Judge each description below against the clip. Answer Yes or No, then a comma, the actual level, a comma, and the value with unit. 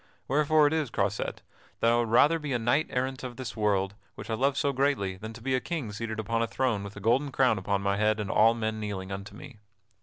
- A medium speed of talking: No, fast, 250 wpm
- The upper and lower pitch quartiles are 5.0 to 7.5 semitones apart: No, average, 4.2 semitones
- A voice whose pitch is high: No, low, 115 Hz